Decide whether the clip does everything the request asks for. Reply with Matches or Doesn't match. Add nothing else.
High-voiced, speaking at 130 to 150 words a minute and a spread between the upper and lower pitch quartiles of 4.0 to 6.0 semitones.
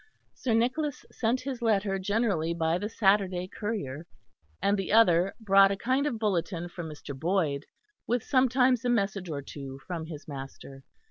Doesn't match